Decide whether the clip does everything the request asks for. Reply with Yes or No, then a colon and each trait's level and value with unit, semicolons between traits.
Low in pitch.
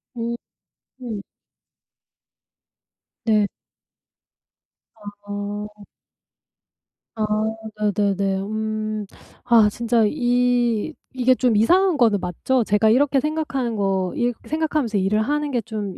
No: high, 225 Hz